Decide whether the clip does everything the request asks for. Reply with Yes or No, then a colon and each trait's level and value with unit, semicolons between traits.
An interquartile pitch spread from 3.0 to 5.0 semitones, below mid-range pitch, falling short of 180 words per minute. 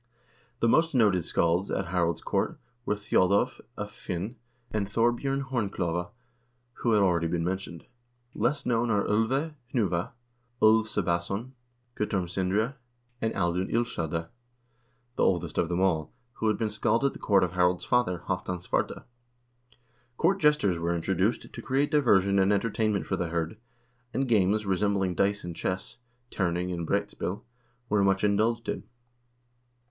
Yes: average, 4.2 semitones; low, 100 Hz; average, 150 wpm